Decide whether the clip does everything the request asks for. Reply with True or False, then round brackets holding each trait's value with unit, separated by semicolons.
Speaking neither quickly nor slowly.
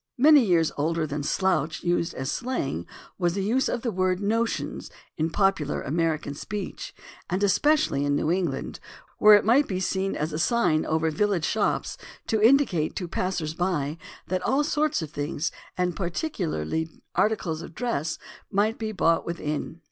True (165 wpm)